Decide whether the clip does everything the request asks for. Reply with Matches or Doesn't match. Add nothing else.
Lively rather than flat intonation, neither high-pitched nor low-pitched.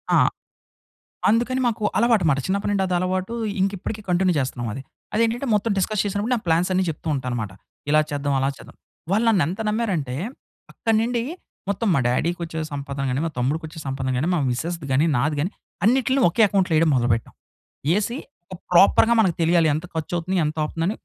Matches